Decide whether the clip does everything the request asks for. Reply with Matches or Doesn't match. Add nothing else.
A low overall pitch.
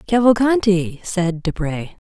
Doesn't match